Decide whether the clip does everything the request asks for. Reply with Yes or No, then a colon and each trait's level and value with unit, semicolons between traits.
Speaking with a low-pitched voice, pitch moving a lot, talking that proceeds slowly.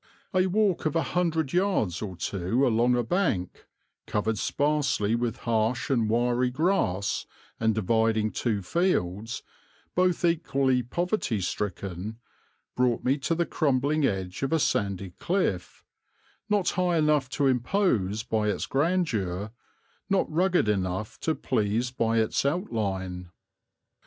Yes: low, 120 Hz; wide, 7.6 semitones; slow, 130 wpm